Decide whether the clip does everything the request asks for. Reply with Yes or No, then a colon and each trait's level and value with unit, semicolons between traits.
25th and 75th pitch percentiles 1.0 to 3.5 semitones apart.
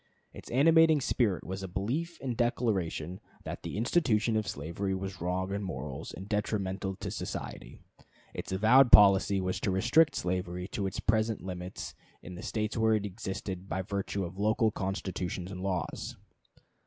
Yes: average, 3.1 semitones